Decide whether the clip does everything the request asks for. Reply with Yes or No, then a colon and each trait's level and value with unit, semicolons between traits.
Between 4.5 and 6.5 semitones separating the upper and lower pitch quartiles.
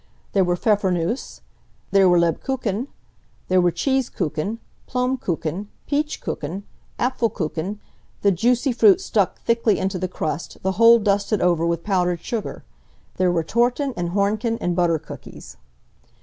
Yes: average, 4.8 semitones